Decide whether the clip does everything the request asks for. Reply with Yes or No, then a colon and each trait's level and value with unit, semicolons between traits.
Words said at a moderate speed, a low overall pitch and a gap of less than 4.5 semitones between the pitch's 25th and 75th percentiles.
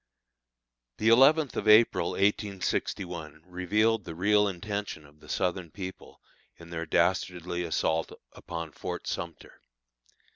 No: slow, 115 wpm; very low, 90 Hz; average, 3.8 semitones